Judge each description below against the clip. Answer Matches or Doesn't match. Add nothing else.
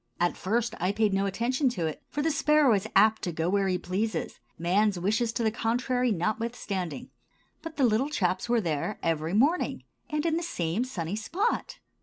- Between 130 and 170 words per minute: Doesn't match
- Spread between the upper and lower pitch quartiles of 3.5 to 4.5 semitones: Doesn't match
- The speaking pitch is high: Matches